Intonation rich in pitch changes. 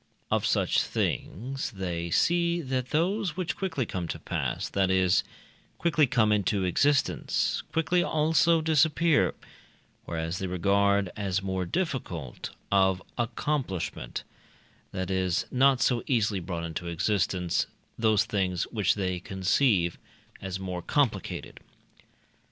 Yes: wide, 7.5 semitones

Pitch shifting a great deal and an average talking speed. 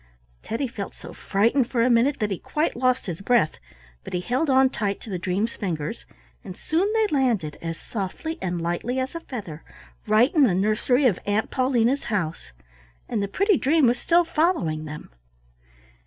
Yes: wide, 6.4 semitones; average, 185 wpm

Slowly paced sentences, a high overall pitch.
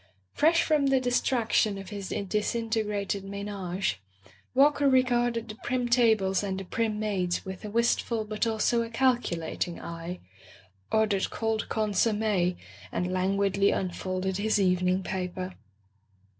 Yes: slow, 130 wpm; high, 210 Hz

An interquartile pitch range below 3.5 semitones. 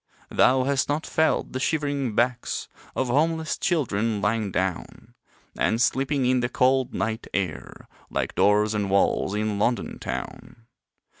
No: average, 4.6 semitones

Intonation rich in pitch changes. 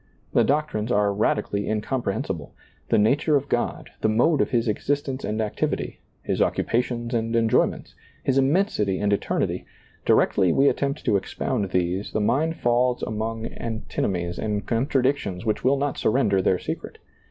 No: average, 4.3 semitones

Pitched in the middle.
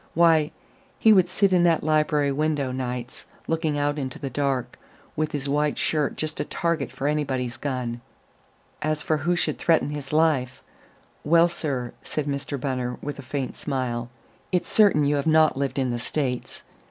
Yes: medium, 145 Hz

